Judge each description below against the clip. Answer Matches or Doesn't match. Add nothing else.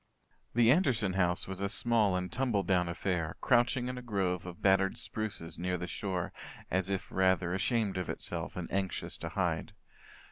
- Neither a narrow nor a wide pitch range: Matches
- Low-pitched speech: Matches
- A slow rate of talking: Doesn't match